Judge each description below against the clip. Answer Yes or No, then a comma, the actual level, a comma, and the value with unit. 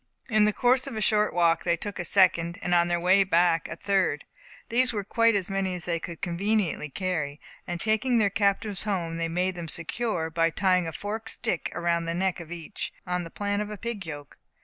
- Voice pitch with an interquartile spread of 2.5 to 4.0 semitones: Yes, average, 3.5 semitones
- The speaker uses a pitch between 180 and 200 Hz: Yes, medium, 185 Hz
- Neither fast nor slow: No, fast, 220 wpm